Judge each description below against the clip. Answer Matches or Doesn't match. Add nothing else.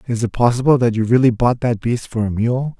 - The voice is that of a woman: Doesn't match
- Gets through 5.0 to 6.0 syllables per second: Matches